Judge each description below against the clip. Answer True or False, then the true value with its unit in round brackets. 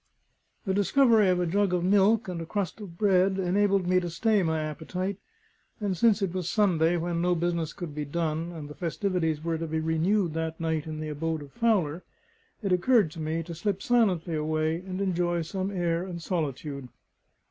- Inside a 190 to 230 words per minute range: True (195 wpm)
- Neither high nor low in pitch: True (175 Hz)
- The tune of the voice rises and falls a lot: False (3.2 semitones)